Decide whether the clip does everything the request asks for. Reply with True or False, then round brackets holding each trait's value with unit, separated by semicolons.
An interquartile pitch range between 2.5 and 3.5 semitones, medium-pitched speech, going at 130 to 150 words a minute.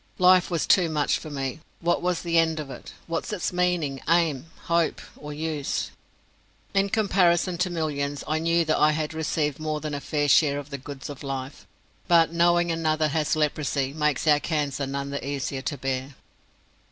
False (2.9 semitones; 155 Hz; 185 wpm)